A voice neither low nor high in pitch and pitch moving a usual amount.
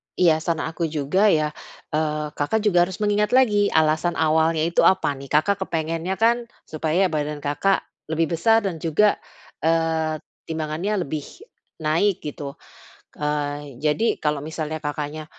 Yes: medium, 160 Hz; average, 3.7 semitones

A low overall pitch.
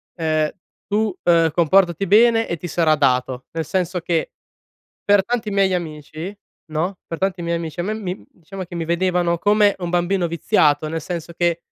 No: medium, 175 Hz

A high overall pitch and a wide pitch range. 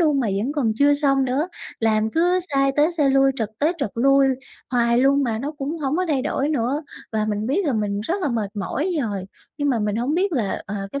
No: very high, 270 Hz; average, 4.7 semitones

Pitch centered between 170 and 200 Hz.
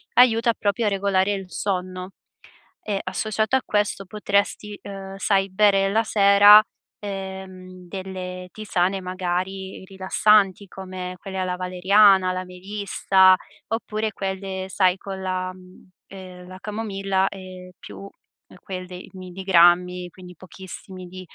Yes: high, 190 Hz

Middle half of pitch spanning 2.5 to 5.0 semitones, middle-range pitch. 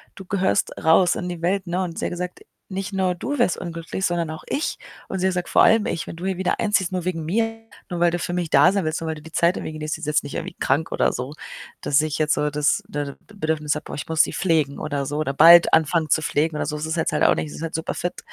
Yes: average, 2.9 semitones; medium, 165 Hz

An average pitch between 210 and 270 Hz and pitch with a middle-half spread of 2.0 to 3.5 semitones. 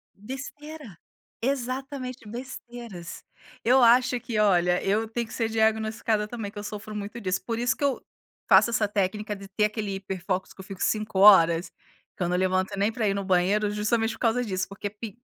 Yes: high, 215 Hz; average, 3.2 semitones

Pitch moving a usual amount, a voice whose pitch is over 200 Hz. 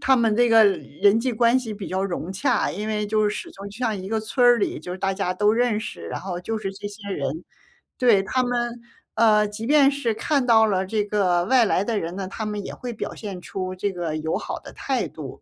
Yes: average, 3.3 semitones; high, 210 Hz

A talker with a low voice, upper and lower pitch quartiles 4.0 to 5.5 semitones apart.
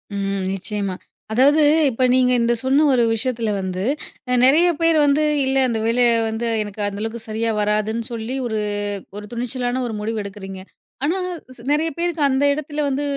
No: high, 235 Hz; average, 4.3 semitones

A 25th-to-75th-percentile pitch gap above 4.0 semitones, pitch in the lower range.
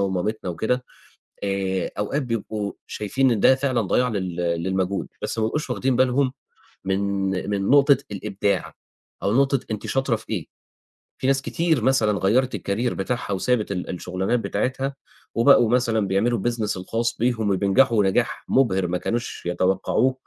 Yes: average, 4.7 semitones; low, 110 Hz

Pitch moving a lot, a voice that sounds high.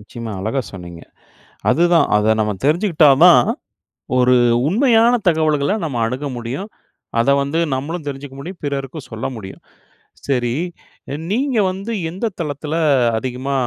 No: wide, 5.7 semitones; medium, 140 Hz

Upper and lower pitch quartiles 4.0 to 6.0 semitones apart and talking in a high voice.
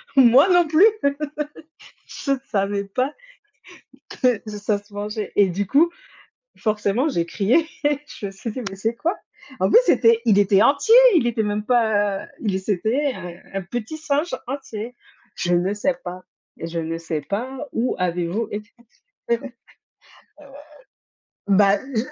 Yes: average, 4.6 semitones; high, 215 Hz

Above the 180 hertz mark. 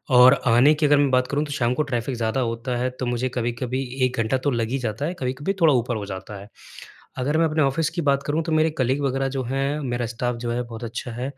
No: low, 130 Hz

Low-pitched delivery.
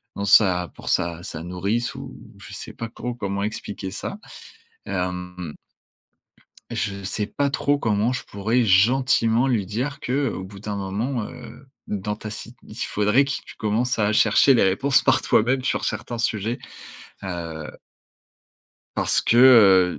Yes: low, 105 Hz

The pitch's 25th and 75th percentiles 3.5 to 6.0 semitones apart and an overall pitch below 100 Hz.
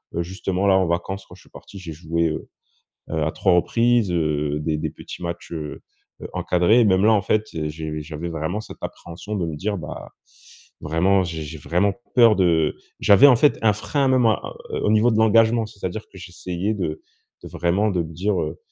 Yes: average, 4.6 semitones; very low, 90 Hz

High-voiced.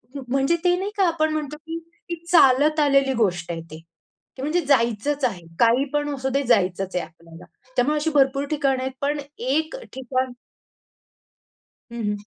Yes: very high, 275 Hz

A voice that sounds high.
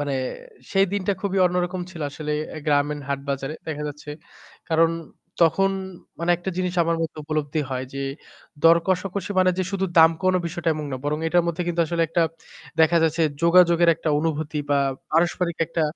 No: medium, 165 Hz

